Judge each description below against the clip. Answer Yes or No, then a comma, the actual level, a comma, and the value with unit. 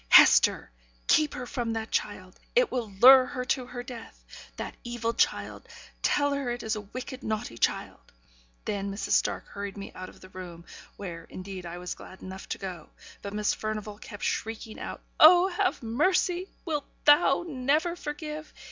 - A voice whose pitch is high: Yes, high, 230 Hz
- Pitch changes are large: Yes, wide, 6.5 semitones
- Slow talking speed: No, average, 175 wpm